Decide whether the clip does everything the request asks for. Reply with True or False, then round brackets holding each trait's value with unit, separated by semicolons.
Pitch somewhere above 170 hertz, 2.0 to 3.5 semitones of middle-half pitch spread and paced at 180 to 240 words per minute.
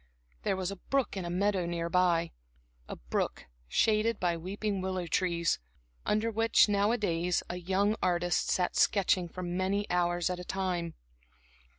False (185 Hz; 2.6 semitones; 155 wpm)